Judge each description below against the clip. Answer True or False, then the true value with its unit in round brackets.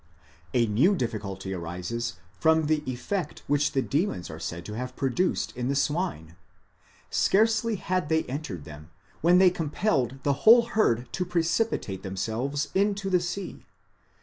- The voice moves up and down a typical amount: False (8.6 semitones)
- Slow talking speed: False (150 wpm)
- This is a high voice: False (145 Hz)